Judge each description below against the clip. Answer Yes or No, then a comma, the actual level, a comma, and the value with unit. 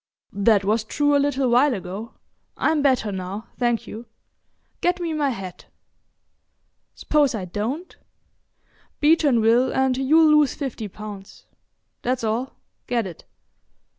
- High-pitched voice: Yes, high, 245 Hz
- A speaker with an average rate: No, slow, 130 wpm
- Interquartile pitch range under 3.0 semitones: No, average, 5.1 semitones